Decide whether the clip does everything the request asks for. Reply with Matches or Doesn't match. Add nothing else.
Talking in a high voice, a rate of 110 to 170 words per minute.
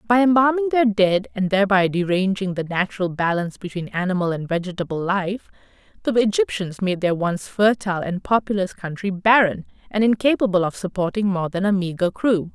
Matches